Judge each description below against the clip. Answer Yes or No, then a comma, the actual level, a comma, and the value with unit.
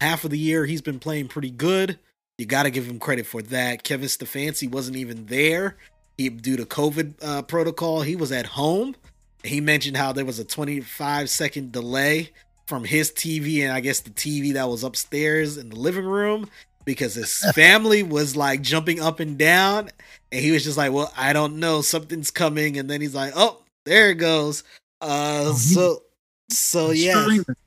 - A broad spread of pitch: No, average, 3.1 semitones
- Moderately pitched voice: Yes, medium, 150 Hz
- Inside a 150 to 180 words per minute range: No, average, 190 wpm